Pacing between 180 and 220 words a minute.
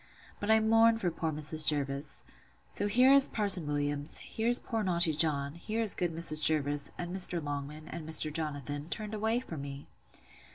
No: average, 170 wpm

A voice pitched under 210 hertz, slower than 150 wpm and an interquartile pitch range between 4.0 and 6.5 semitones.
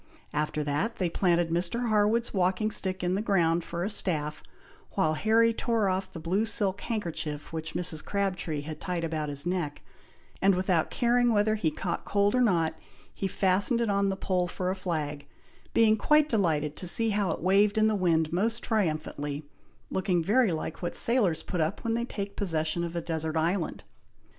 No: medium, 185 Hz; average, 185 wpm; average, 4.3 semitones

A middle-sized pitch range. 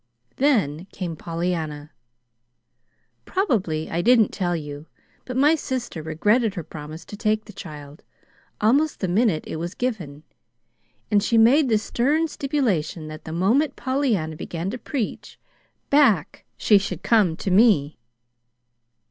No: wide, 7.4 semitones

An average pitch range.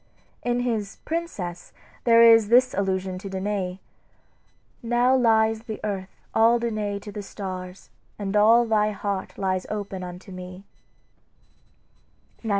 Yes: average, 3.3 semitones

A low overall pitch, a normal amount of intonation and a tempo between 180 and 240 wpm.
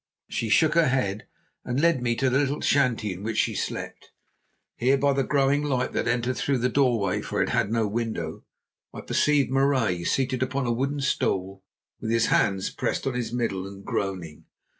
Yes: low, 125 Hz; average, 4.4 semitones; average, 190 wpm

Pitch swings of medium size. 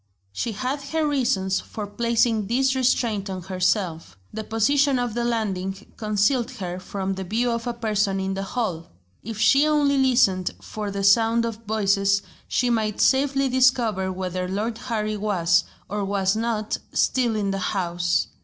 Yes: average, 3.8 semitones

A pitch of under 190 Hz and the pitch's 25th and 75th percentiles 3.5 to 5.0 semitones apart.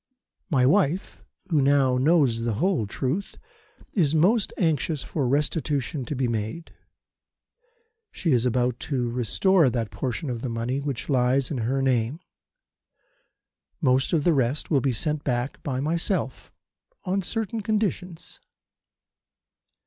Yes: medium, 140 Hz; average, 4.7 semitones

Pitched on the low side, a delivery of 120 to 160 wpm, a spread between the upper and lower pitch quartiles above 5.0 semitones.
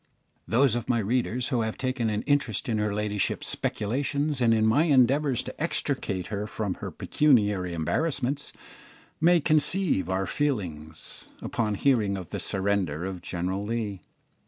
Yes: low, 110 Hz; average, 150 wpm; wide, 5.6 semitones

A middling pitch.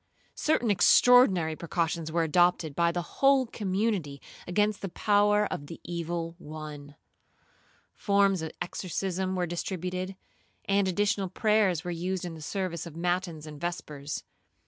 Yes: medium, 180 Hz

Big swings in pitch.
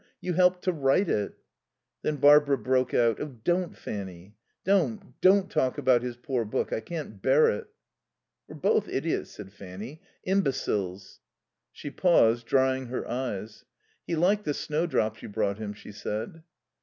Yes: wide, 7.2 semitones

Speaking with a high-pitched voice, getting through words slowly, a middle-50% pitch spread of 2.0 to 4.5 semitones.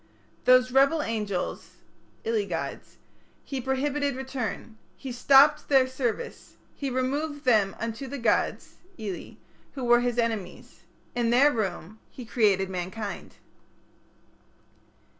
Yes: high, 245 Hz; slow, 115 wpm; average, 3.6 semitones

